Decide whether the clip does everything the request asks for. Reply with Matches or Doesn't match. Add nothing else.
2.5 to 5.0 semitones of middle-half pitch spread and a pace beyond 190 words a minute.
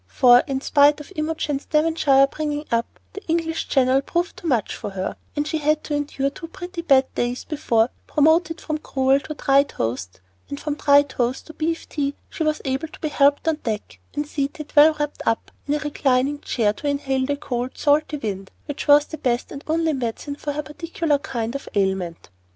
Matches